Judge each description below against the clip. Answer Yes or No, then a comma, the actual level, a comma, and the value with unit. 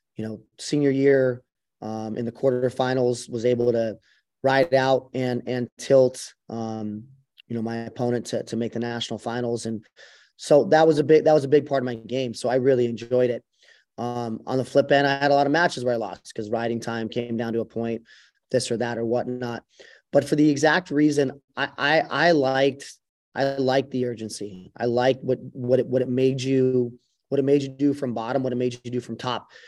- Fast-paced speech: Yes, fast, 220 wpm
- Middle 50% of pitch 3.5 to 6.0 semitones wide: No, narrow, 2.5 semitones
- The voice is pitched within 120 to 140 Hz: Yes, low, 125 Hz